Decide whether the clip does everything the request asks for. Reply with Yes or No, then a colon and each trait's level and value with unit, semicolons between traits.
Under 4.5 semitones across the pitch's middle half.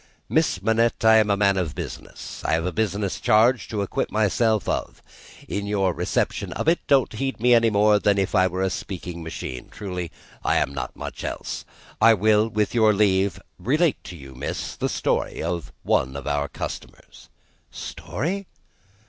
Yes: average, 3.7 semitones